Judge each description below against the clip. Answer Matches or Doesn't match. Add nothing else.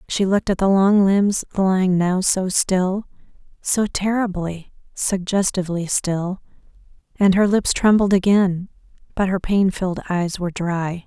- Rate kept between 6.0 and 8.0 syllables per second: Doesn't match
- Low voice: Doesn't match